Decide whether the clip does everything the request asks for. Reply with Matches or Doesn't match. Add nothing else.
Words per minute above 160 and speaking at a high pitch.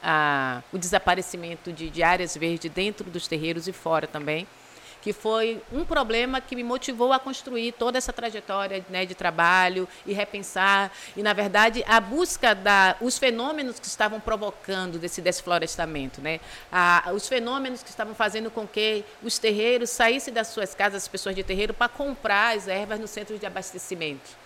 Matches